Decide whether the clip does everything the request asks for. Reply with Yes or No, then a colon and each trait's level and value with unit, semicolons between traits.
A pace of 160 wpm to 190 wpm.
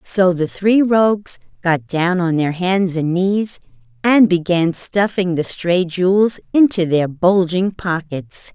No: average, 145 wpm